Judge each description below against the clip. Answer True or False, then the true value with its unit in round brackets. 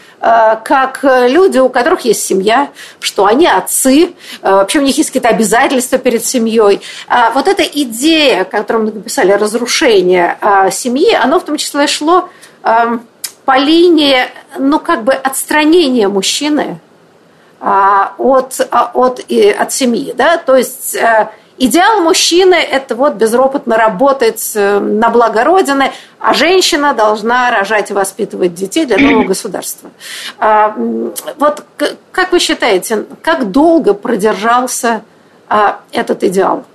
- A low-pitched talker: False (255 Hz)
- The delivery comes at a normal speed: True (120 wpm)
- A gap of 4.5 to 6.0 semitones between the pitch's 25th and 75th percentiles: True (5.6 semitones)